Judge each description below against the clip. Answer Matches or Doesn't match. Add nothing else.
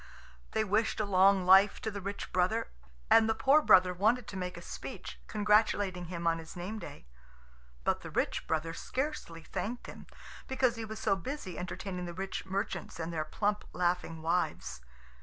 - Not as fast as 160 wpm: Doesn't match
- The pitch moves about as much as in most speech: Matches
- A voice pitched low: Doesn't match